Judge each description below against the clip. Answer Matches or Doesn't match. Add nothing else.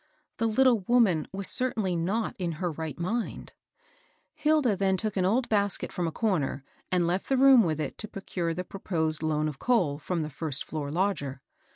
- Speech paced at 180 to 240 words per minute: Matches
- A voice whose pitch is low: Doesn't match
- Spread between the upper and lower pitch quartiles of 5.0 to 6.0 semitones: Matches